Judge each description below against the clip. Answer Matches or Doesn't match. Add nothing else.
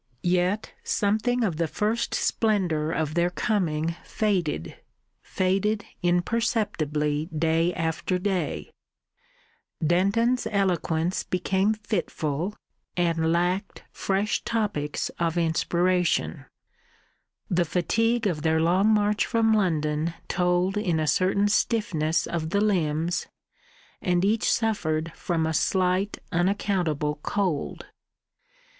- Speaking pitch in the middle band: Matches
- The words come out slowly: Matches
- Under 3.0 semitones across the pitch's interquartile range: Doesn't match